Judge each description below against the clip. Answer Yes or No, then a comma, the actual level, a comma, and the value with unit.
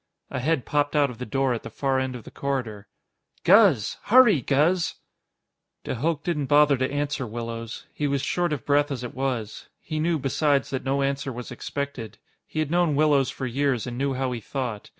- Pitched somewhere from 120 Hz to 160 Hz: Yes, low, 135 Hz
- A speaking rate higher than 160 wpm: Yes, fast, 205 wpm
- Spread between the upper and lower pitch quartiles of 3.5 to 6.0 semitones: No, average, 2.9 semitones